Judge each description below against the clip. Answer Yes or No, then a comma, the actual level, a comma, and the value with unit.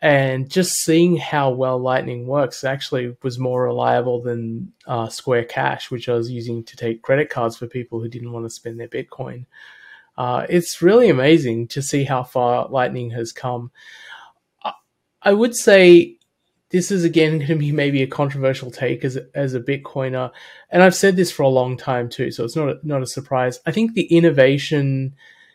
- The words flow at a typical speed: Yes, average, 195 wpm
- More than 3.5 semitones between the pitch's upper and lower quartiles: Yes, average, 4.5 semitones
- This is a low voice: Yes, low, 130 Hz